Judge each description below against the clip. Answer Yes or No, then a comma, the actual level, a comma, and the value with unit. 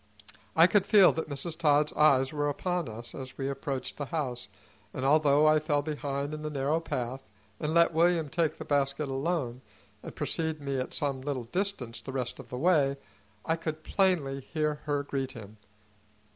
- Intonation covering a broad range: No, average, 3.0 semitones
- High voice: No, medium, 145 Hz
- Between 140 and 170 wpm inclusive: No, average, 185 wpm